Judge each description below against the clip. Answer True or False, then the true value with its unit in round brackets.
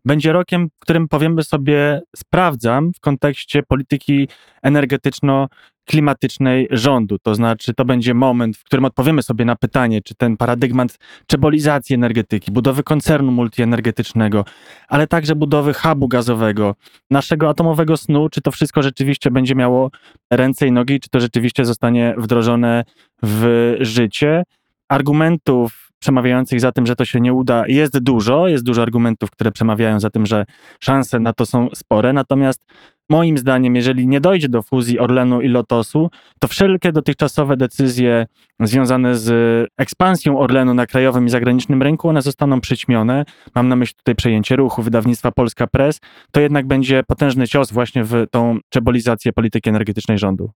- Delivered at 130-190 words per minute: True (150 wpm)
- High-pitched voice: False (130 Hz)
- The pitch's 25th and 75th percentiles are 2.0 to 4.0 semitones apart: True (3.3 semitones)